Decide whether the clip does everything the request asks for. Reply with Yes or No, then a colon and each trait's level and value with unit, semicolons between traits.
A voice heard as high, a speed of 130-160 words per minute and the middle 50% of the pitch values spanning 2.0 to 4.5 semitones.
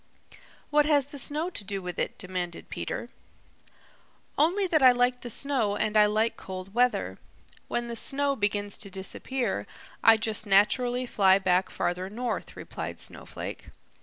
No: high, 225 Hz; average, 155 wpm; average, 5.1 semitones